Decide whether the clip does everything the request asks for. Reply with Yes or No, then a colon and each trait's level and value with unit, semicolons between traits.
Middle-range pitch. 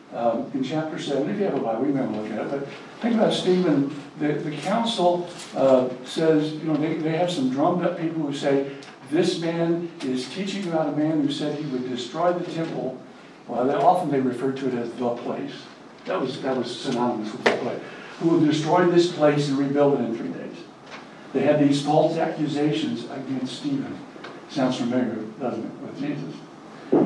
Yes: medium, 150 Hz